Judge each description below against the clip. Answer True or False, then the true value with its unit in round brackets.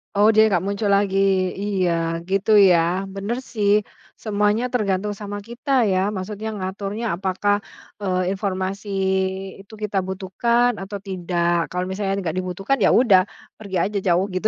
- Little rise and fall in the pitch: True (2.0 semitones)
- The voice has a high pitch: True (195 Hz)